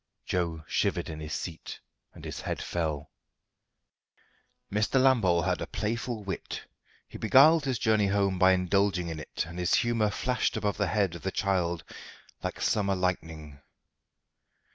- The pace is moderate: Yes, average, 150 wpm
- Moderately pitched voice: No, very low, 95 Hz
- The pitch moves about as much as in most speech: Yes, average, 3.9 semitones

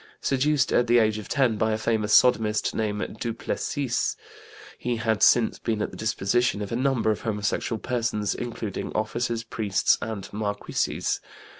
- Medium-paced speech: Yes, average, 155 wpm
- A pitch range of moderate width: No, narrow, 2.2 semitones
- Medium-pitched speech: No, low, 110 Hz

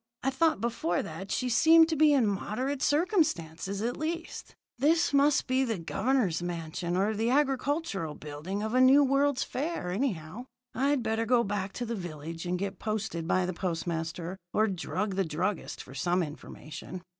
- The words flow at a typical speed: Yes, average, 170 wpm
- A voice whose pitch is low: No, high, 210 Hz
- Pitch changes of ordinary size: No, wide, 7.3 semitones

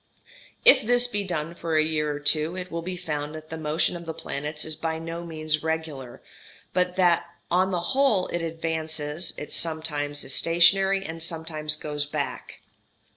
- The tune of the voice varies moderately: No, narrow, 2.2 semitones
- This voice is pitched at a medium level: Yes, medium, 160 Hz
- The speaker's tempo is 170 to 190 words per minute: Yes, average, 180 wpm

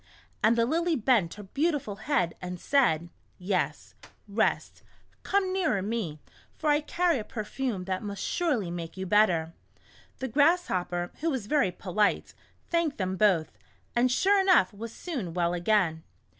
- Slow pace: No, average, 155 wpm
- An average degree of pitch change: No, wide, 8.1 semitones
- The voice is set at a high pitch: Yes, high, 215 Hz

